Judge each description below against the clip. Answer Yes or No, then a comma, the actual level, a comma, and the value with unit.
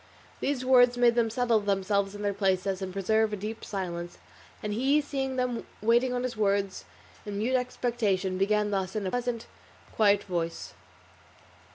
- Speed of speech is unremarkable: Yes, average, 165 wpm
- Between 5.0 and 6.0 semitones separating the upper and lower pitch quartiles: No, average, 3.8 semitones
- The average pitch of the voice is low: No, high, 210 Hz